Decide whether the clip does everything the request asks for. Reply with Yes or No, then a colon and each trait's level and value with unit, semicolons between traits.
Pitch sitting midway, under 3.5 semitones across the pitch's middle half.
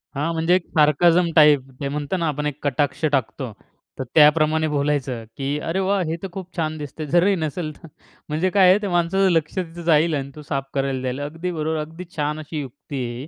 Yes: medium, 155 Hz; average, 2.9 semitones